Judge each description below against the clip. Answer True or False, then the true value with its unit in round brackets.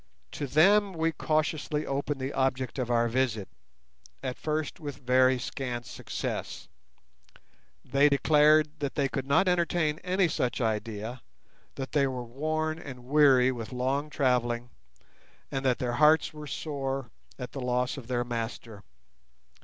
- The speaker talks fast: False (145 wpm)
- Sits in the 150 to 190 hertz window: False (135 Hz)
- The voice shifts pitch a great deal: False (3.4 semitones)